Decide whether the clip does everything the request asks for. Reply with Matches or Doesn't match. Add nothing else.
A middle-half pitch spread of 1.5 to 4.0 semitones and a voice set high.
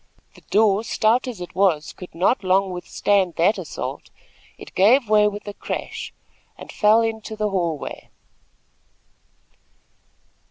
Matches